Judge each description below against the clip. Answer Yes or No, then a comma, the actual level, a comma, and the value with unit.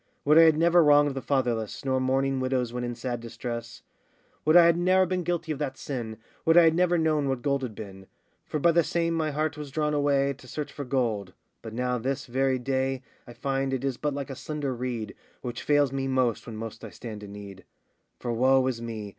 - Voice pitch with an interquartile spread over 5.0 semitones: No, average, 3.8 semitones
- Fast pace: Yes, fast, 230 wpm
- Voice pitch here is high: No, low, 135 Hz